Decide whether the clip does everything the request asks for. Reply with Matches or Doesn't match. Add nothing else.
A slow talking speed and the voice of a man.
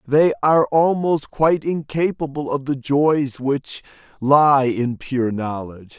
Matches